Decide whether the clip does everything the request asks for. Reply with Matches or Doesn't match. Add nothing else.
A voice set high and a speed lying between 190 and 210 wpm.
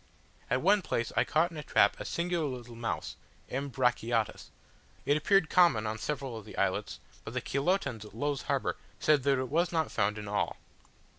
Doesn't match